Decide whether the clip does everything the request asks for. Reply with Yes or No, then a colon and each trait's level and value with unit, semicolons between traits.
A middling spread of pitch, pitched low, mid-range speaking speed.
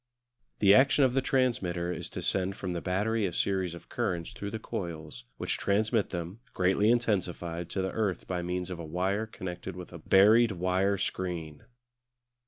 Yes: average, 3.1 semitones; very low, 95 Hz; average, 180 wpm